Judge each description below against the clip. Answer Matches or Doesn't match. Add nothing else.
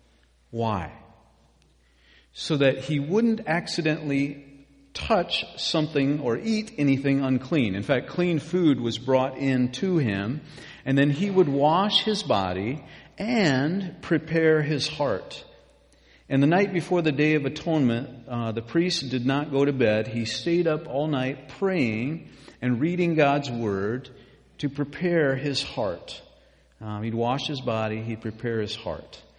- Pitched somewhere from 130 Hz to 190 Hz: Matches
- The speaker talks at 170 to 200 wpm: Doesn't match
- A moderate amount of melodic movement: Doesn't match